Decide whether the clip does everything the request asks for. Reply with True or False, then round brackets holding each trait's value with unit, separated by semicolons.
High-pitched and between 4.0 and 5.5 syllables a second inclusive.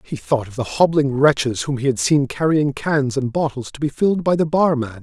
False (140 Hz; 5.3 syllables/s)